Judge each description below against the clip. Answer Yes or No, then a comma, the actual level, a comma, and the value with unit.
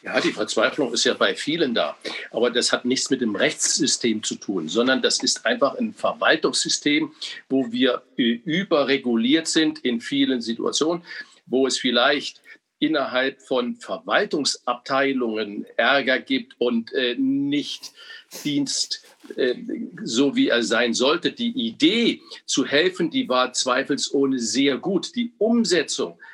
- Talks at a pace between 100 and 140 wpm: Yes, average, 135 wpm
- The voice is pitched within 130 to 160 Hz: Yes, medium, 140 Hz